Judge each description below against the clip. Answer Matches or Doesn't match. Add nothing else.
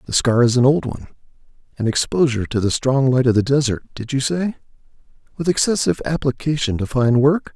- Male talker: Matches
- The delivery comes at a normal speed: Matches